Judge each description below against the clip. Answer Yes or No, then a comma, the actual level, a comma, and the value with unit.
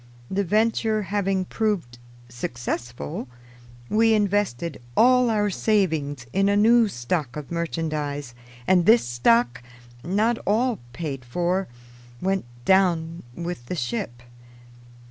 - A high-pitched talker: No, medium, 180 Hz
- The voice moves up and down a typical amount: No, wide, 7.2 semitones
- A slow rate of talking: Yes, slow, 110 wpm